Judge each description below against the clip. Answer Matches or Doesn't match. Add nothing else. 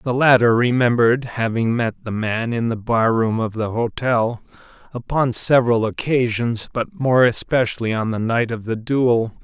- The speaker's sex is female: Doesn't match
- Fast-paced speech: Doesn't match